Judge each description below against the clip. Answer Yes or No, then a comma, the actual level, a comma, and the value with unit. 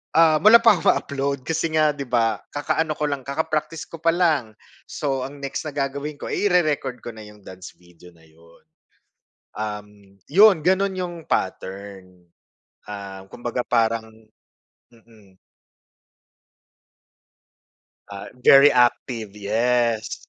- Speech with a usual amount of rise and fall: No, wide, 6.7 semitones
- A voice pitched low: Yes, low, 130 Hz